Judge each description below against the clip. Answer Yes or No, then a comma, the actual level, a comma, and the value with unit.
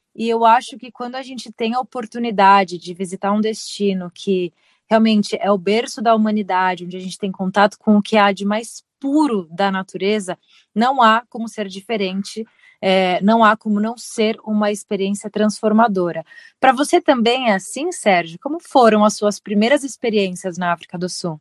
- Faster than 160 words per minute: Yes, average, 180 wpm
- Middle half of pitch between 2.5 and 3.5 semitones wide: Yes, average, 3.0 semitones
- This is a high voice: Yes, high, 210 Hz